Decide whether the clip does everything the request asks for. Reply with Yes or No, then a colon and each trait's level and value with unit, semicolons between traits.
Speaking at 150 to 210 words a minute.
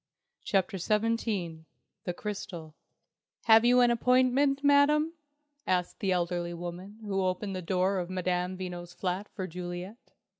No: slow, 135 wpm